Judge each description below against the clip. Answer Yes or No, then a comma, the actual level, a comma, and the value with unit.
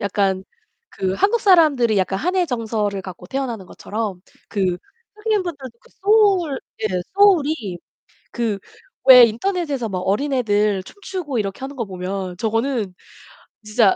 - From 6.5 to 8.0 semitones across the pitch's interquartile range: Yes, wide, 7.7 semitones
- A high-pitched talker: Yes, high, 230 Hz